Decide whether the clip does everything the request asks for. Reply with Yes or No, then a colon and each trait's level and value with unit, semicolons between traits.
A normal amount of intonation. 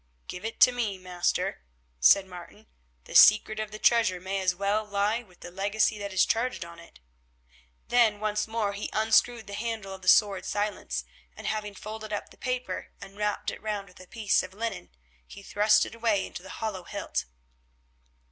No: narrow, 2.3 semitones